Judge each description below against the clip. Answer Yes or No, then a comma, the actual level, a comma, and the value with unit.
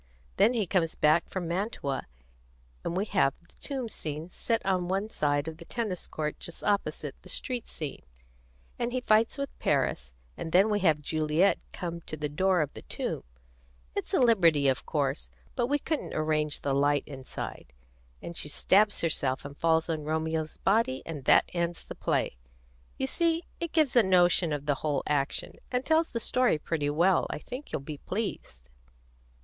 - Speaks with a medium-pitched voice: Yes, medium, 170 Hz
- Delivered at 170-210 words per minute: Yes, average, 180 wpm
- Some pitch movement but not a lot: No, wide, 6.1 semitones